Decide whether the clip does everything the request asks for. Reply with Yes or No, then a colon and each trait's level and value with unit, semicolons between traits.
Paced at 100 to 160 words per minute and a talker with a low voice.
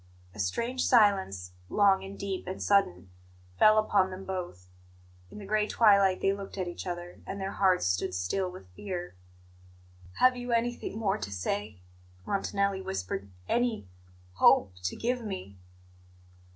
No: average, 150 wpm; high, 190 Hz